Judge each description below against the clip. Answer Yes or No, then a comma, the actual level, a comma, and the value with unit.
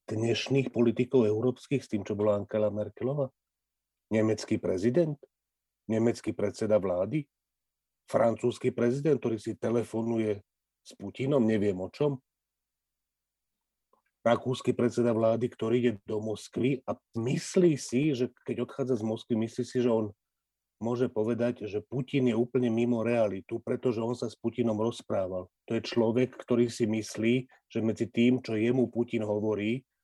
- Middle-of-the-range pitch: No, low, 115 Hz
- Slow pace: No, average, 140 wpm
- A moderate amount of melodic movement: No, narrow, 2.3 semitones